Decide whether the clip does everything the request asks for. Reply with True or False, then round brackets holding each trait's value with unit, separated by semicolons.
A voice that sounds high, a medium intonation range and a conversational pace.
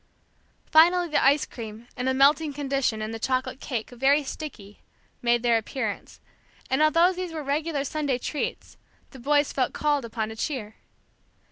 True (270 Hz; 4.1 semitones; 160 wpm)